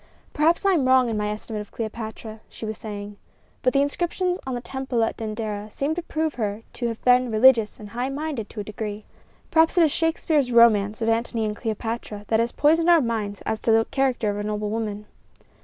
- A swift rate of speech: Yes, fast, 215 wpm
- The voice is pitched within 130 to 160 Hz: No, high, 230 Hz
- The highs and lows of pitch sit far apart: No, average, 4.2 semitones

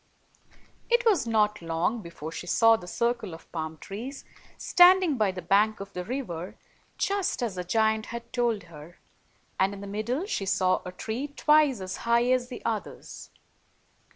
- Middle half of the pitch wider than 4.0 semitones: Yes, average, 5.1 semitones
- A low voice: No, high, 220 Hz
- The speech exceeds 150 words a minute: Yes, average, 170 wpm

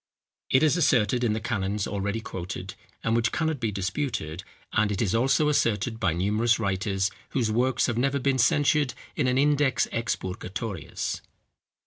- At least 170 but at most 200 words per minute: No, average, 155 wpm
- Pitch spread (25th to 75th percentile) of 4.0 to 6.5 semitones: Yes, average, 4.7 semitones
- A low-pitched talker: Yes, low, 115 Hz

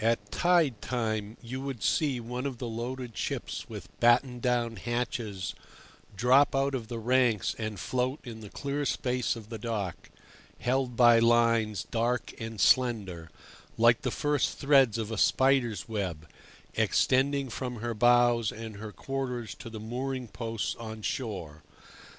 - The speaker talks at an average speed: Yes, average, 150 wpm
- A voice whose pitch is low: Yes, low, 120 Hz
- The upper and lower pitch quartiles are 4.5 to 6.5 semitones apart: No, average, 2.7 semitones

